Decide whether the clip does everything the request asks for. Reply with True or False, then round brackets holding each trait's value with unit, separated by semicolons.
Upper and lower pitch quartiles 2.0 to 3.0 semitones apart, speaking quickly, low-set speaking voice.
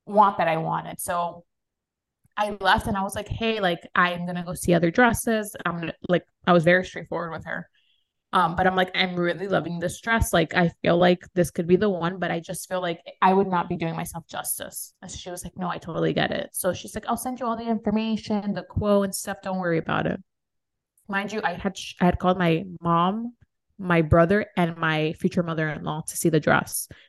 False (2.6 semitones; 230 wpm; 180 Hz)